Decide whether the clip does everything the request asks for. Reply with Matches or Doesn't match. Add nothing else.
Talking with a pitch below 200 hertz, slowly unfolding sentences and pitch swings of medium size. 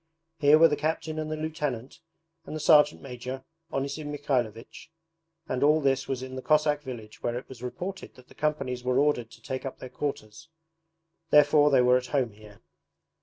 Doesn't match